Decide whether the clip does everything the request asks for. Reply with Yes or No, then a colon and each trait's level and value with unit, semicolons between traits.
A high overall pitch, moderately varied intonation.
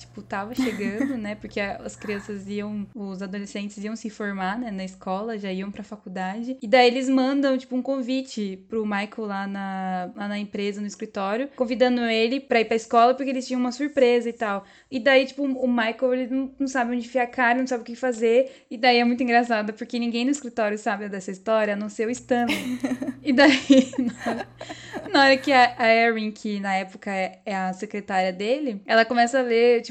Yes: high, 235 Hz; average, 3.7 semitones